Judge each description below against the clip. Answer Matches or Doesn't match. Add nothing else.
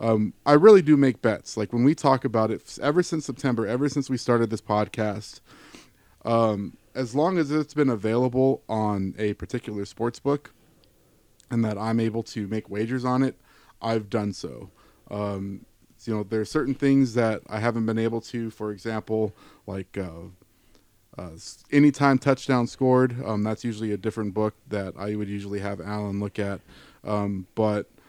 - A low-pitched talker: Matches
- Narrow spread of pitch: Doesn't match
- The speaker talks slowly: Doesn't match